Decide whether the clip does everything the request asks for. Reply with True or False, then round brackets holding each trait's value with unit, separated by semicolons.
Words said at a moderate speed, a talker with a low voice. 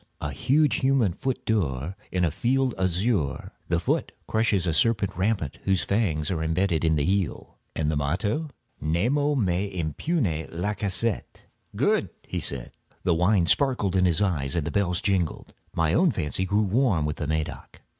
True (165 wpm; 95 Hz)